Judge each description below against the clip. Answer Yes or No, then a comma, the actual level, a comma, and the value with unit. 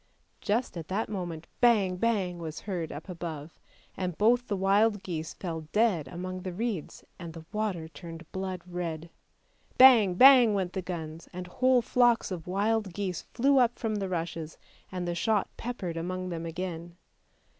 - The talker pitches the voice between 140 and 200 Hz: Yes, medium, 185 Hz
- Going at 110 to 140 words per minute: No, average, 165 wpm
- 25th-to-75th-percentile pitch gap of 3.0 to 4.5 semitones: Yes, average, 4.1 semitones